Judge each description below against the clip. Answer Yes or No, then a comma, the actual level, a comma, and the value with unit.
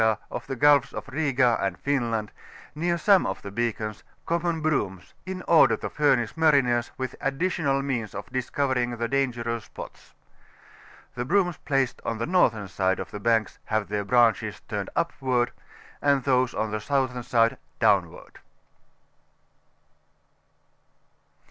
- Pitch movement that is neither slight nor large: Yes, average, 3.9 semitones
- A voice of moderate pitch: No, low, 125 Hz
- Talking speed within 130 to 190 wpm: Yes, slow, 135 wpm